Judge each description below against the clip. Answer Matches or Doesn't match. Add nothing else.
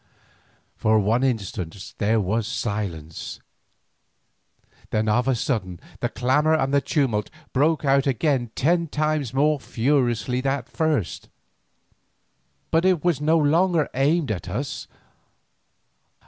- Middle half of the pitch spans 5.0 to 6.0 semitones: Matches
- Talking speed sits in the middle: Doesn't match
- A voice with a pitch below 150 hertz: Matches